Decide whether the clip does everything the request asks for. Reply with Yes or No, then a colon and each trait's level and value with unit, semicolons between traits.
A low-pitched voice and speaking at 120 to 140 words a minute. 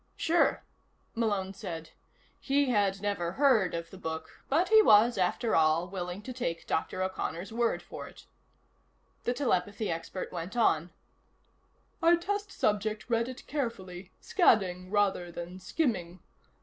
No: high, 200 Hz; slow, 135 wpm